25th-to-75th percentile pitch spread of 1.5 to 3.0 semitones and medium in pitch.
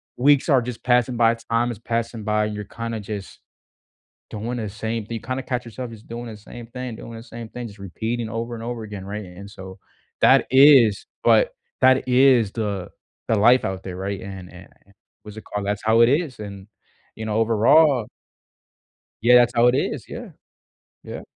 No: average, 2.7 semitones; low, 115 Hz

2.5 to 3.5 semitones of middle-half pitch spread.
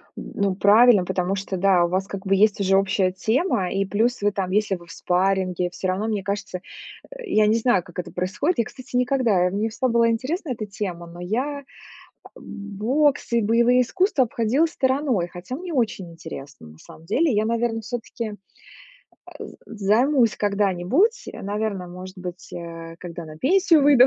No: average, 5.0 semitones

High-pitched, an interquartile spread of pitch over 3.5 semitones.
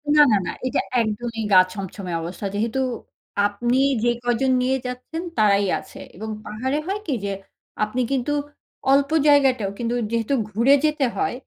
Yes: high, 240 Hz; average, 4.1 semitones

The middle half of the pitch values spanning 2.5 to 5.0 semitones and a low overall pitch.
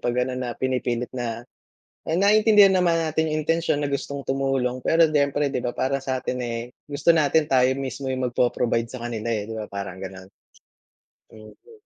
Yes: average, 4.1 semitones; low, 130 Hz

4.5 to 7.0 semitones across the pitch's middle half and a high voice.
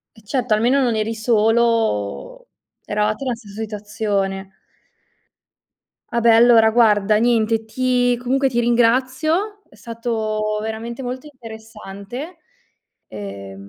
No: narrow, 2.6 semitones; high, 225 Hz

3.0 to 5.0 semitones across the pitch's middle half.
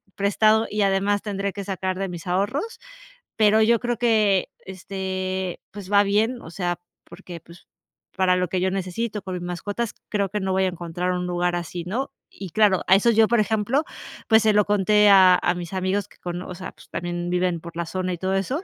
No: narrow, 2.6 semitones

